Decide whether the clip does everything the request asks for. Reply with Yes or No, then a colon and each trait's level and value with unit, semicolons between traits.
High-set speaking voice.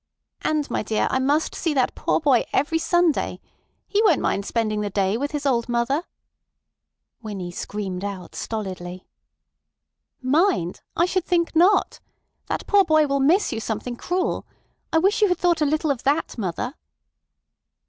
Yes: very high, 275 Hz